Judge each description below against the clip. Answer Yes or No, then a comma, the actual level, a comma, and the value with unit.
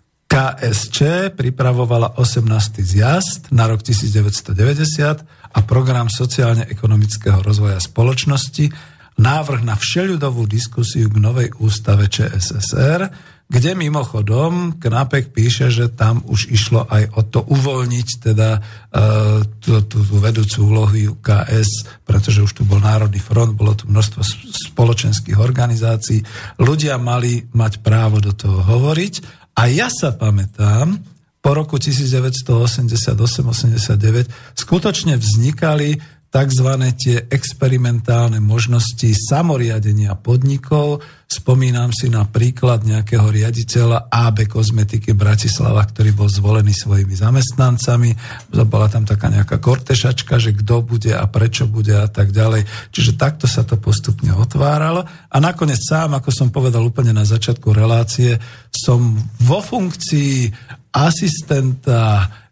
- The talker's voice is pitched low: Yes, low, 120 Hz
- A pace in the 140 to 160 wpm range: No, average, 115 wpm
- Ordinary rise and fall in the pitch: Yes, average, 3.4 semitones